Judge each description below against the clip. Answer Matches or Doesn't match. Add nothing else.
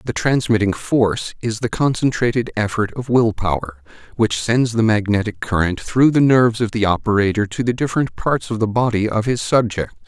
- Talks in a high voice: Doesn't match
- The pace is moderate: Matches